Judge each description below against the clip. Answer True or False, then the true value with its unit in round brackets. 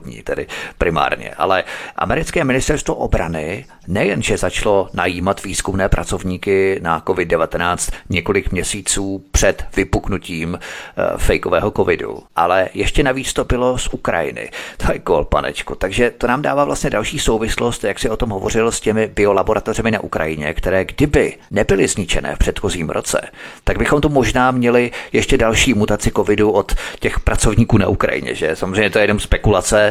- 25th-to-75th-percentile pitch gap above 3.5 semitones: True (4.3 semitones)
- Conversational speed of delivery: True (150 wpm)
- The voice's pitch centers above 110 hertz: False (105 Hz)